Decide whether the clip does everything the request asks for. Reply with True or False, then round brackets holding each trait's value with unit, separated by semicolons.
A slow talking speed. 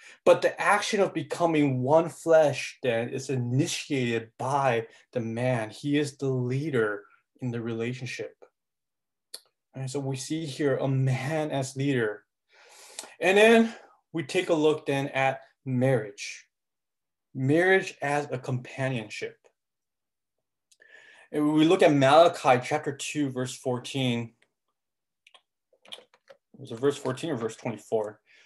True (120 wpm)